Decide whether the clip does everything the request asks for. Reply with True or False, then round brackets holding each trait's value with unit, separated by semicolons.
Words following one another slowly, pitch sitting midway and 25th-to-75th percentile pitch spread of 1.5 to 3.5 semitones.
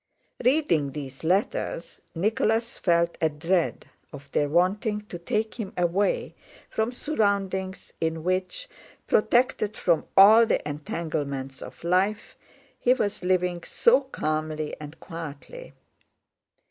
False (115 wpm; 180 Hz; 5.2 semitones)